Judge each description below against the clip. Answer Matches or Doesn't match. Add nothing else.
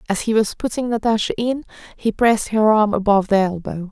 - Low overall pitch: Doesn't match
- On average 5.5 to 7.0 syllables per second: Matches